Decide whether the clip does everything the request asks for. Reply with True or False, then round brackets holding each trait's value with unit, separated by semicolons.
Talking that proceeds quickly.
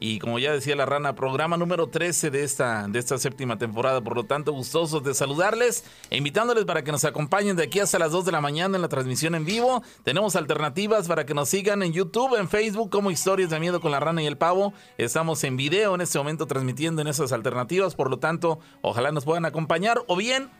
True (230 wpm)